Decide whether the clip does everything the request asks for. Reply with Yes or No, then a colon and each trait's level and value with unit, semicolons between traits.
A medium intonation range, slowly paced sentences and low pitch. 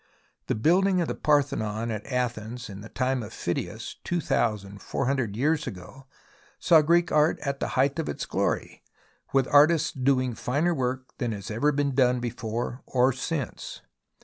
No: average, 4.3 semitones; average, 170 wpm; low, 130 Hz